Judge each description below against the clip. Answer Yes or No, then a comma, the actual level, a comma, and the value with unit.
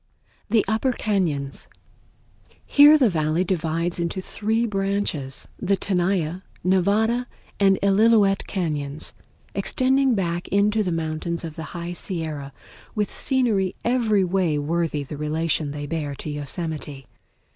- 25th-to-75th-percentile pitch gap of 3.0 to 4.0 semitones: No, average, 4.7 semitones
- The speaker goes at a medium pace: No, slow, 125 wpm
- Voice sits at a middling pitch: Yes, medium, 180 Hz